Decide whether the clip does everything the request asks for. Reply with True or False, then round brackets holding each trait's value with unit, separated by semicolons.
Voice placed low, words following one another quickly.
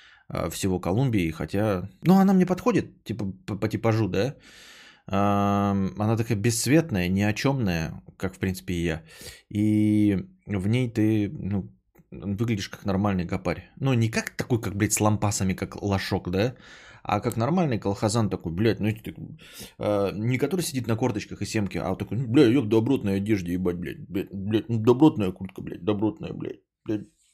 True (105 Hz; 170 wpm)